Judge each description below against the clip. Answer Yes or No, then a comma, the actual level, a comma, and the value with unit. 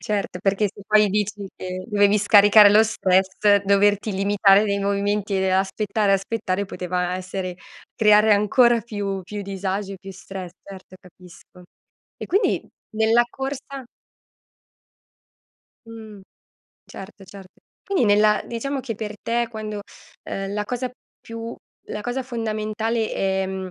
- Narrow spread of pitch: Yes, narrow, 2.2 semitones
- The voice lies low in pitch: No, high, 205 Hz